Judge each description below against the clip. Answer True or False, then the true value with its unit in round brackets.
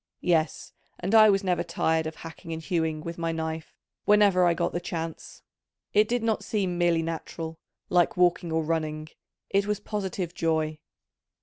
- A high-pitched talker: False (170 Hz)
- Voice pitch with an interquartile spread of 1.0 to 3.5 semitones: True (2.9 semitones)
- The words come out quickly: False (170 wpm)